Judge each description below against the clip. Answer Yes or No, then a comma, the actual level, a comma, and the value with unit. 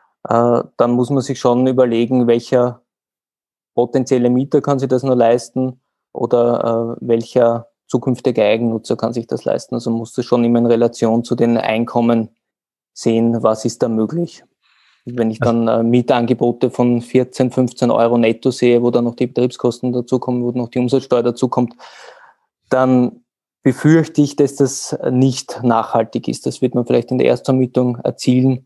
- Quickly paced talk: No, average, 160 wpm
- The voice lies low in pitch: Yes, low, 120 Hz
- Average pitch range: No, narrow, 1.6 semitones